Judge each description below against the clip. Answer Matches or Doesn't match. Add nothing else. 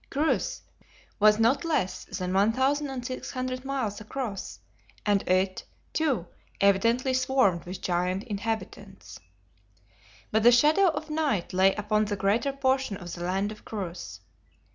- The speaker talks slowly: Matches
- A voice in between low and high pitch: Doesn't match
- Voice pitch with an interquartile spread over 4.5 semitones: Matches